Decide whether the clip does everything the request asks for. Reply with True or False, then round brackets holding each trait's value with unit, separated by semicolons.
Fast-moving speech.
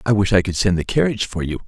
True (320 wpm)